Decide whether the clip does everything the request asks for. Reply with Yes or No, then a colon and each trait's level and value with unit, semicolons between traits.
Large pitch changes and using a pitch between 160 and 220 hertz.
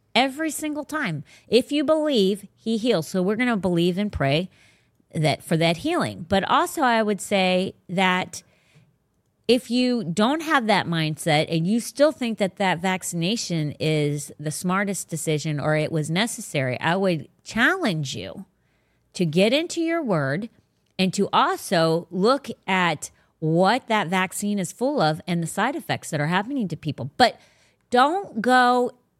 Yes: wide, 6.5 semitones; high, 190 Hz